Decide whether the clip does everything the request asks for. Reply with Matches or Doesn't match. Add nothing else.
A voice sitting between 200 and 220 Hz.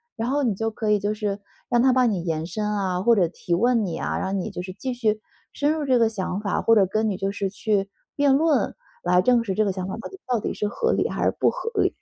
Matches